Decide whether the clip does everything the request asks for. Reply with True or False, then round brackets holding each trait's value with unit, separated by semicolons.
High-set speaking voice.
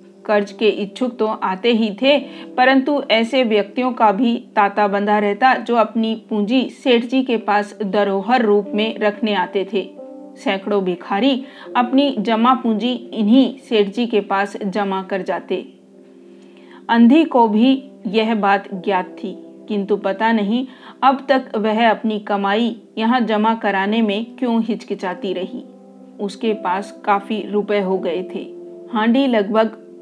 True (215 Hz)